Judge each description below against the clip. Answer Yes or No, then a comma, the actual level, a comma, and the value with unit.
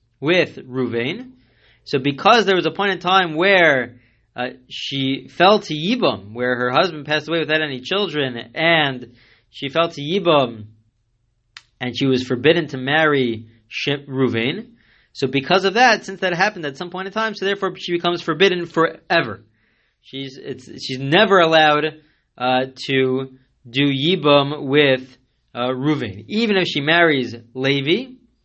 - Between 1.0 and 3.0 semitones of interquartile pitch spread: No, average, 5.3 semitones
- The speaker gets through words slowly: No, average, 150 wpm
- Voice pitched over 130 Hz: Yes, medium, 140 Hz